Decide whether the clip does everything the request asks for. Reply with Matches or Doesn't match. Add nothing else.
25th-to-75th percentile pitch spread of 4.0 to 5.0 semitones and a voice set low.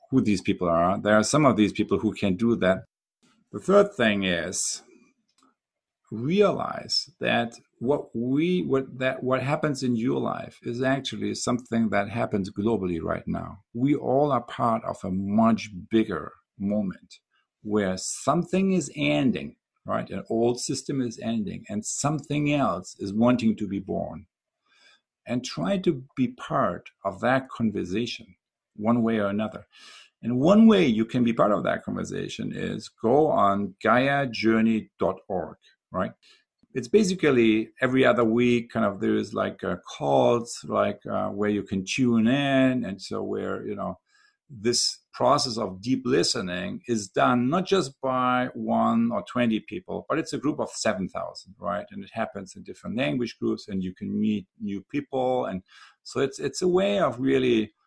Matches